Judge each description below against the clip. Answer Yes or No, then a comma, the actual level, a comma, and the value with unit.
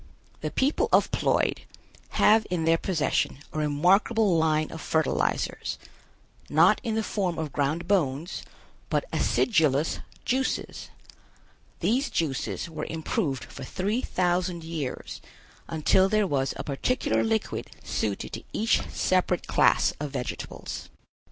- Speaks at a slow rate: Yes, slow, 125 wpm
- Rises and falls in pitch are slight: No, average, 5.2 semitones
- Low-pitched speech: No, medium, 170 Hz